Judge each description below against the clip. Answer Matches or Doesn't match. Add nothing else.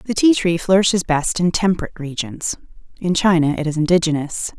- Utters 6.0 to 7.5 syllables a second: Doesn't match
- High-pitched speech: Doesn't match